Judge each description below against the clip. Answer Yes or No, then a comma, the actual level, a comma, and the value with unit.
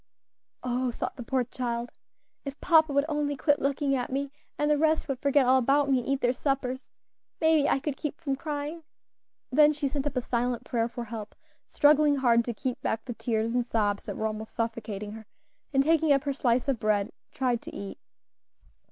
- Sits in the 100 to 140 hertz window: No, very high, 265 Hz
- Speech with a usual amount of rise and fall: Yes, average, 3.5 semitones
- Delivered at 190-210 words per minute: Yes, fast, 205 wpm